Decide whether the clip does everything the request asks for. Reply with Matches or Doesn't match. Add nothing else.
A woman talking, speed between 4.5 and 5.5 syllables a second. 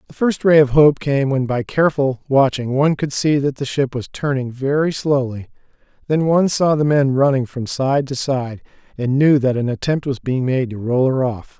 Doesn't match